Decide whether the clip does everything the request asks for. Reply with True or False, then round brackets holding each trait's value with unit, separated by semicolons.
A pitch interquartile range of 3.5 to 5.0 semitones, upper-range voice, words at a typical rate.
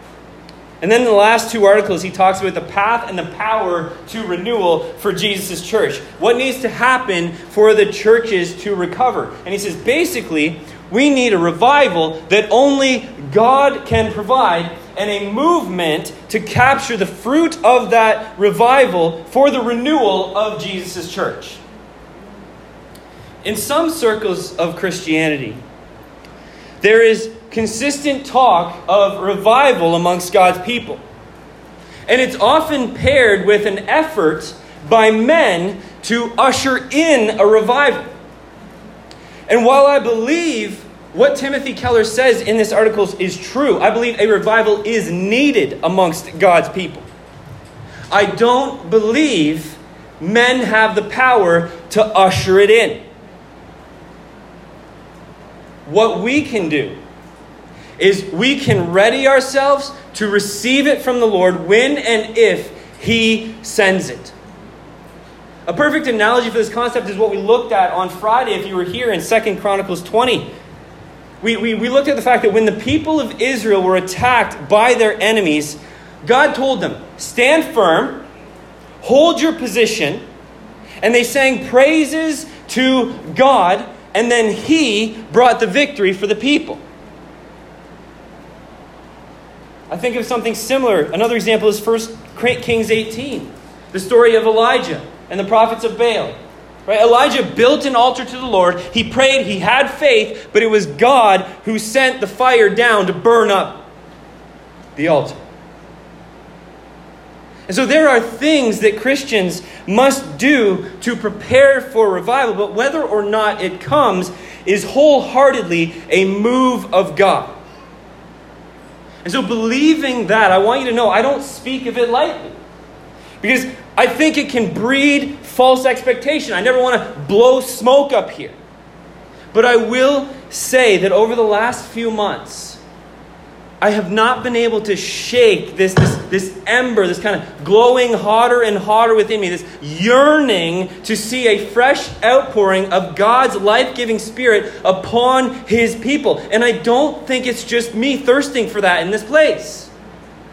True (4.5 semitones; 225 Hz; 145 wpm)